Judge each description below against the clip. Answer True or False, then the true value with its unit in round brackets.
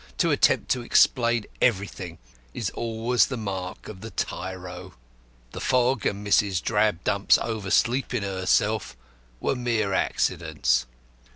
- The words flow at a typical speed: False (115 wpm)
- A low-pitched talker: True (105 Hz)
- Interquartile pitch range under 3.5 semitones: False (3.9 semitones)